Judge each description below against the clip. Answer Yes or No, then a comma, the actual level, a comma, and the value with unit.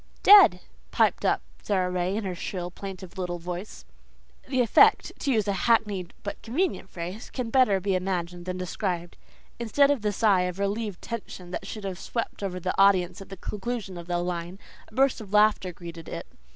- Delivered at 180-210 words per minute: Yes, average, 190 wpm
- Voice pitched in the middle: No, high, 195 Hz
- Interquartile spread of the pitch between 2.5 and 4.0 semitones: Yes, average, 3.2 semitones